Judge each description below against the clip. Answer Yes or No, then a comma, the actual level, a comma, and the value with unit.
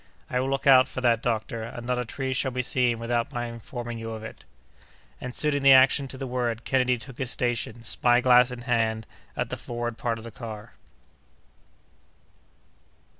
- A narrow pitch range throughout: Yes, narrow, 1.8 semitones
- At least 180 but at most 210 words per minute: Yes, average, 190 wpm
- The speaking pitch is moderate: No, low, 120 Hz